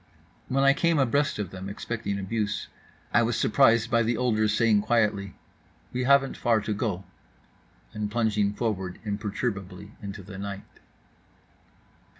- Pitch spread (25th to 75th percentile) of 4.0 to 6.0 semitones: No, average, 2.8 semitones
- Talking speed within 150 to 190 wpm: No, average, 140 wpm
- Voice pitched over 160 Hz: No, low, 110 Hz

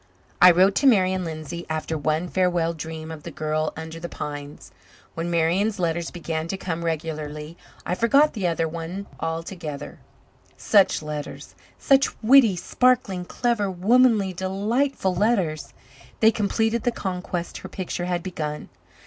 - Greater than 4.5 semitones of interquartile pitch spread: No, average, 3.8 semitones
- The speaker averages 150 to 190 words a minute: No, average, 140 wpm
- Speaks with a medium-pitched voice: Yes, medium, 175 Hz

